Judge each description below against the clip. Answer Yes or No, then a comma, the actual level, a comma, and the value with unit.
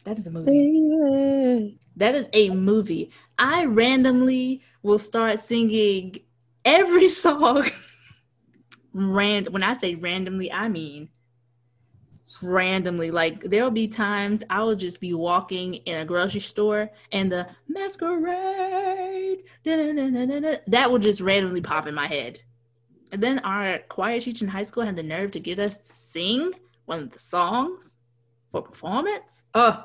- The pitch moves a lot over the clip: Yes, wide, 6.6 semitones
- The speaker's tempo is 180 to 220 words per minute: No, average, 140 wpm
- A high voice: Yes, high, 205 Hz